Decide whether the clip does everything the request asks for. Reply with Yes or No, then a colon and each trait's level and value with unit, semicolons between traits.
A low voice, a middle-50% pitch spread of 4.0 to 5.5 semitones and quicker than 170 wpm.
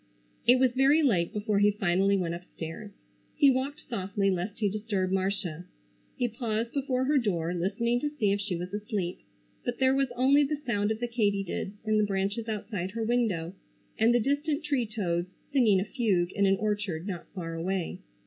No: high, 210 Hz; average, 4.4 semitones; average, 185 wpm